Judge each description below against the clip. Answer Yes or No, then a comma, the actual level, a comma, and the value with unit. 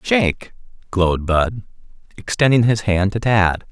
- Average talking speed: No, slow, 130 wpm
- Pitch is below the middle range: Yes, low, 105 Hz